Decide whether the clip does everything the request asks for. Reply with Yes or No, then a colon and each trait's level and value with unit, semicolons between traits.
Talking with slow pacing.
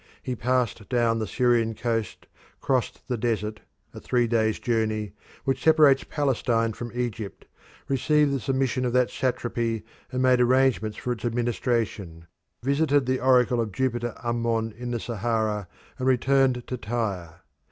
No: average, 145 wpm